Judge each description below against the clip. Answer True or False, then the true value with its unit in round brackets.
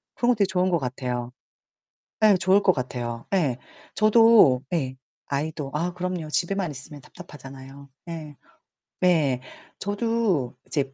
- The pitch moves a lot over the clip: True (5.8 semitones)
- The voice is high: False (160 Hz)